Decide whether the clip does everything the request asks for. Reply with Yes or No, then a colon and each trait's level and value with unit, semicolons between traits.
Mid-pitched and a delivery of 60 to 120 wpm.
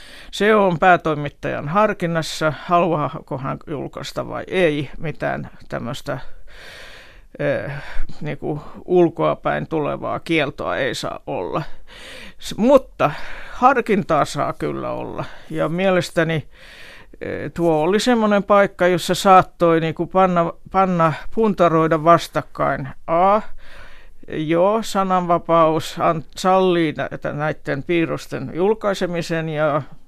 Yes: medium, 170 Hz; average, 100 wpm